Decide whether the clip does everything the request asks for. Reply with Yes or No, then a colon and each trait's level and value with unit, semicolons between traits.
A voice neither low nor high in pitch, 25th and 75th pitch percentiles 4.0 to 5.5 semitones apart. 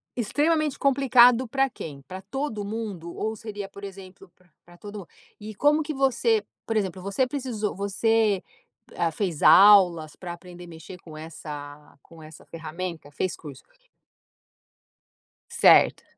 No: high, 195 Hz; average, 5.1 semitones